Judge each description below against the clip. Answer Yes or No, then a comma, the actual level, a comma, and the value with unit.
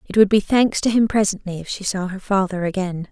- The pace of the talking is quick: Yes, fast, 250 wpm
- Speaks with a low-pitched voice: No, high, 195 Hz